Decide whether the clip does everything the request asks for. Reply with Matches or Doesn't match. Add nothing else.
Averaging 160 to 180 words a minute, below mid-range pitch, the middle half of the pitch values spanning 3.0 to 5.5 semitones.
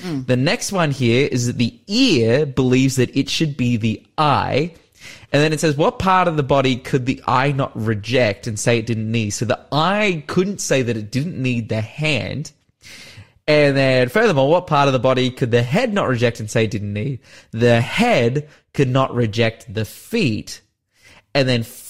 Doesn't match